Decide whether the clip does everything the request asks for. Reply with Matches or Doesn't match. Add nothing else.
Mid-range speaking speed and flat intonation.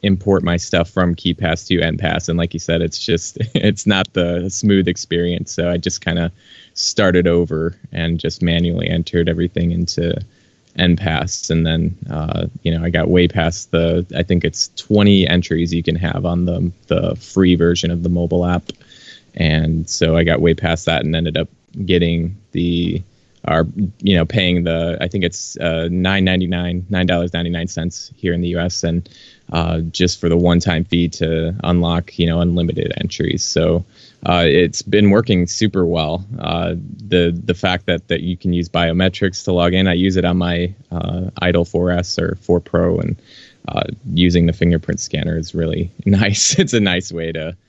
Matches